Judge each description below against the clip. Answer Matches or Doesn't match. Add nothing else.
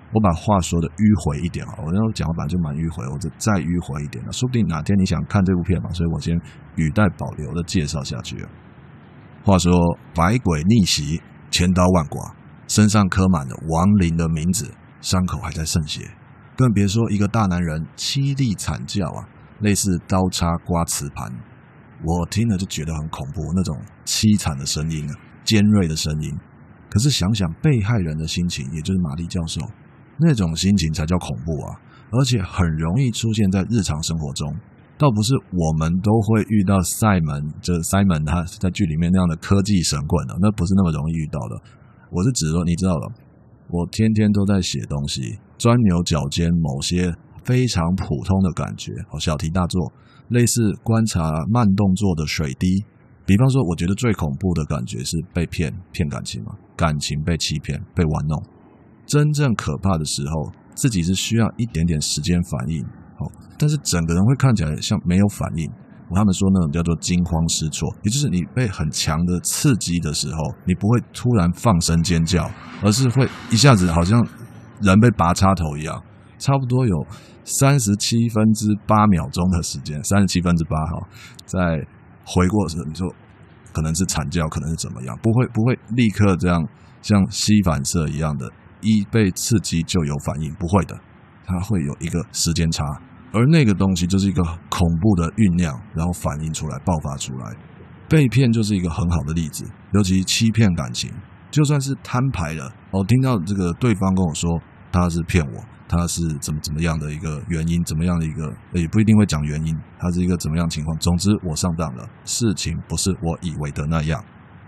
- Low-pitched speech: Matches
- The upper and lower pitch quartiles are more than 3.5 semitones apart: Matches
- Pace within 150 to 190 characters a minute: Doesn't match